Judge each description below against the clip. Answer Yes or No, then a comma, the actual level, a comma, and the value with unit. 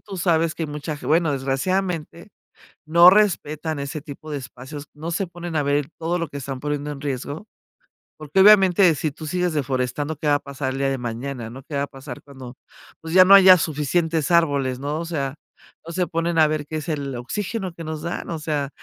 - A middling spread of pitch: Yes, average, 3.3 semitones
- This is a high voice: No, medium, 155 Hz